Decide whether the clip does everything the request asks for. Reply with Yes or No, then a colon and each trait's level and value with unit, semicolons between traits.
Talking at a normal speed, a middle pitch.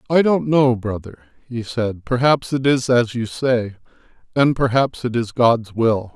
No: average, 175 wpm; low, 120 Hz